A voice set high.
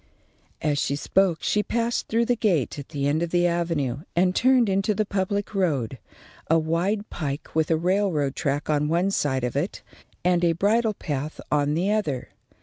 No: medium, 170 Hz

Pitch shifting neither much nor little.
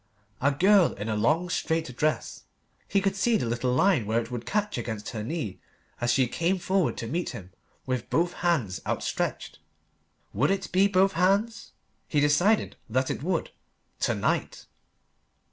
No: wide, 7.9 semitones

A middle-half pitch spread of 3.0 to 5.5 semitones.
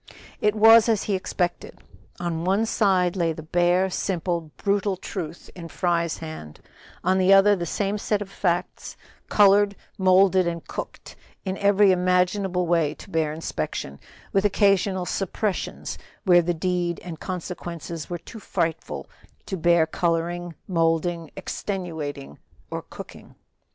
No: narrow, 2.6 semitones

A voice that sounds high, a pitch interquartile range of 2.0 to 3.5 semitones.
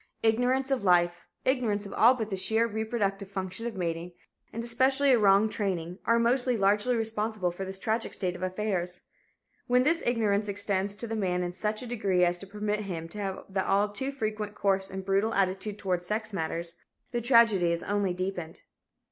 Yes: high, 205 Hz; average, 3.2 semitones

